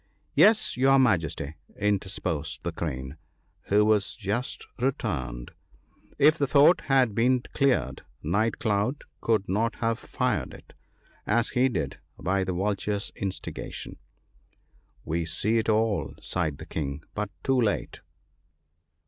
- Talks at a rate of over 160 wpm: No, average, 140 wpm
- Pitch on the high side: No, low, 105 Hz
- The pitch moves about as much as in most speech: No, wide, 6.0 semitones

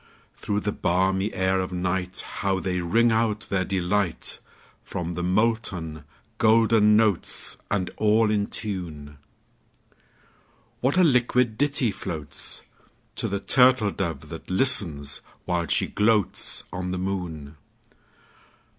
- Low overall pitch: Yes, very low, 95 Hz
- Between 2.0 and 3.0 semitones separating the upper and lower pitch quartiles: No, average, 3.8 semitones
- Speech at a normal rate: No, slow, 100 wpm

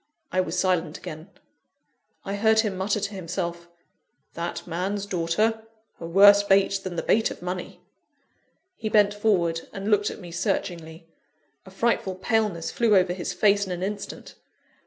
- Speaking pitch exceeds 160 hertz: Yes, high, 190 Hz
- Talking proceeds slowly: No, average, 155 wpm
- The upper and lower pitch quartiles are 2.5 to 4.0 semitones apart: Yes, average, 2.9 semitones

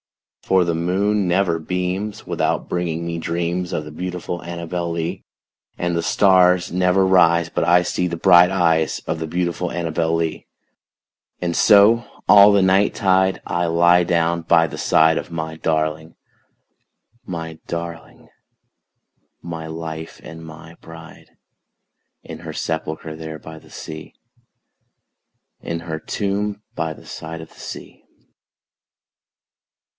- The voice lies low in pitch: Yes, very low, 85 Hz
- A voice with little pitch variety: Yes, narrow, 1.8 semitones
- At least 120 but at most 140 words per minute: Yes, slow, 135 wpm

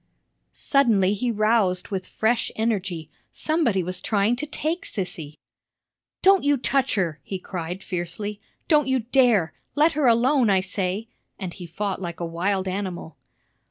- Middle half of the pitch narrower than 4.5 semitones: No, average, 5.3 semitones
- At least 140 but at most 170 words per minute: Yes, average, 150 wpm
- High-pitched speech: Yes, high, 205 Hz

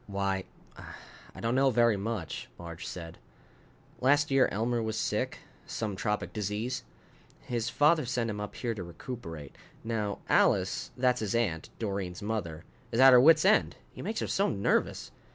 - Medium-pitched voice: No, low, 110 Hz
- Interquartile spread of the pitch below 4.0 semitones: No, average, 4.3 semitones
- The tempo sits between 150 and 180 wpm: Yes, average, 160 wpm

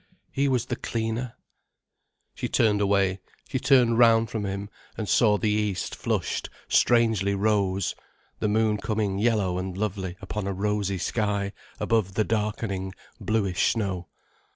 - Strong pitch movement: No, narrow, 2.4 semitones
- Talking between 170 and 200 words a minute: No, average, 140 wpm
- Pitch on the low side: Yes, low, 105 Hz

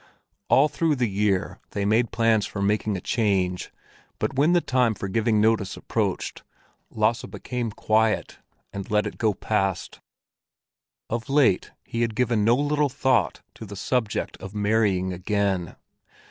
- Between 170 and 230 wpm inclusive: No, average, 150 wpm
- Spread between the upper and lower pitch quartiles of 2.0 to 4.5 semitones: Yes, average, 3.1 semitones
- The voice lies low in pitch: Yes, low, 110 Hz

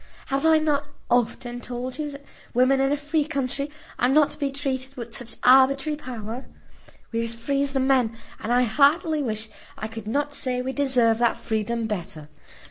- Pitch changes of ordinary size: Yes, average, 3.3 semitones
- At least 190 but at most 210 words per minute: Yes, average, 195 wpm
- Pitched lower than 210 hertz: No, very high, 260 Hz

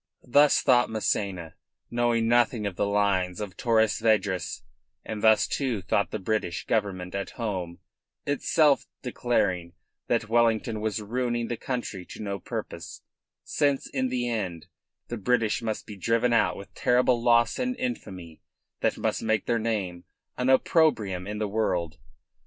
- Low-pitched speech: Yes, low, 110 Hz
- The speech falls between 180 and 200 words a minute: No, average, 150 wpm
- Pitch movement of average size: Yes, average, 3.5 semitones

